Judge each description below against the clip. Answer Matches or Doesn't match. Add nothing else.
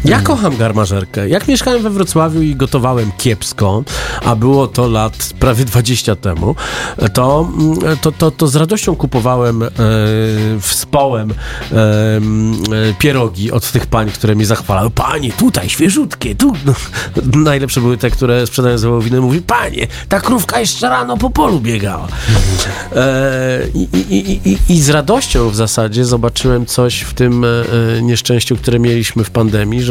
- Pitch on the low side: Matches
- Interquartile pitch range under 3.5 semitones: Doesn't match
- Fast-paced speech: Doesn't match